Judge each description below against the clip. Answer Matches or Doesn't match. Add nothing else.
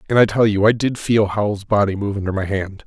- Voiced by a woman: Doesn't match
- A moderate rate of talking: Doesn't match